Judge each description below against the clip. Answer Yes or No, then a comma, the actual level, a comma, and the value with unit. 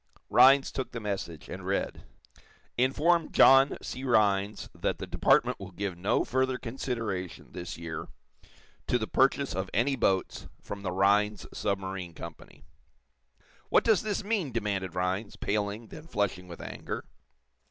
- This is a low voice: Yes, low, 105 Hz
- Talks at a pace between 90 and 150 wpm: Yes, average, 140 wpm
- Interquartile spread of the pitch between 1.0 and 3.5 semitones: No, wide, 5.6 semitones